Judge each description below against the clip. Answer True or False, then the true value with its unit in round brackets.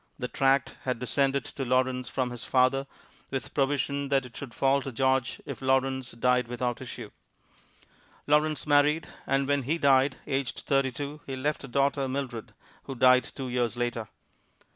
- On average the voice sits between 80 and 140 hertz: True (135 Hz)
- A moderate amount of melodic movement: False (1.7 semitones)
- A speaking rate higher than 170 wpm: False (165 wpm)